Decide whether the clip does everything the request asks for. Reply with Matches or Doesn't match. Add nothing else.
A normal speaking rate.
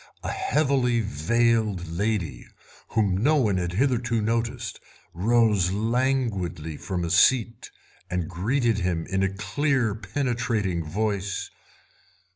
Doesn't match